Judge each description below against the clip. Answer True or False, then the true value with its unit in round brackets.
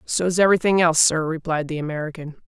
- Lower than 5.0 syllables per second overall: False (6.5 syllables/s)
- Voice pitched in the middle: True (165 Hz)